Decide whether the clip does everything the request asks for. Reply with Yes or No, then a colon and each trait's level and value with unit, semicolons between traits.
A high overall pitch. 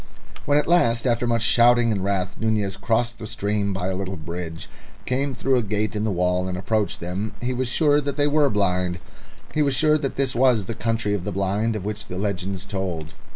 No: low, 105 Hz